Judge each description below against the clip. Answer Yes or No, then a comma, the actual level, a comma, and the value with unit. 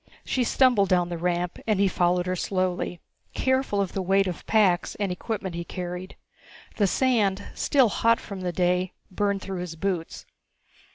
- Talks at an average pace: Yes, average, 170 wpm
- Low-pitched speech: No, medium, 185 Hz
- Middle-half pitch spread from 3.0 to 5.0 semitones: No, narrow, 2.4 semitones